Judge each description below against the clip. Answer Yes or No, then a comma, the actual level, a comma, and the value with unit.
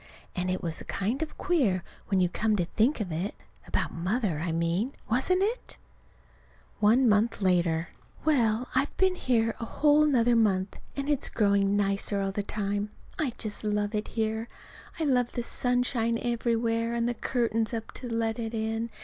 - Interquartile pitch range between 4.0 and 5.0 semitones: No, average, 3.6 semitones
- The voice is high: Yes, high, 225 Hz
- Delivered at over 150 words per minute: Yes, average, 170 wpm